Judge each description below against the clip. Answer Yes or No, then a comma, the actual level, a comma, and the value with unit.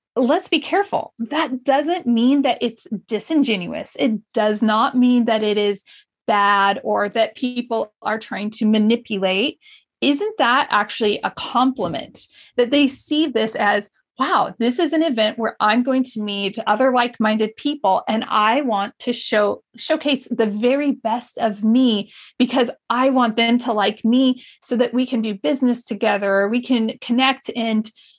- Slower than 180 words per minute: Yes, average, 160 wpm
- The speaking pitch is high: Yes, high, 235 Hz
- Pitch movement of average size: Yes, average, 3.5 semitones